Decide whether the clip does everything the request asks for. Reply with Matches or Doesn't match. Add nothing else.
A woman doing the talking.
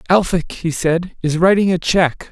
Doesn't match